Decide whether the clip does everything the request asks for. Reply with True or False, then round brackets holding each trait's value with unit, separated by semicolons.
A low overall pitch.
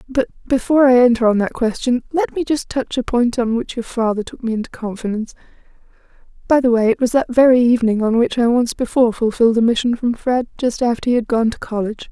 False (240 Hz)